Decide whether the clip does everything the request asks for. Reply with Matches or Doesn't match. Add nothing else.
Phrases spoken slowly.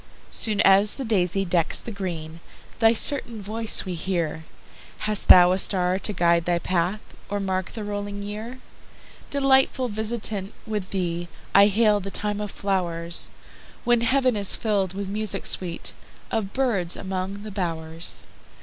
Matches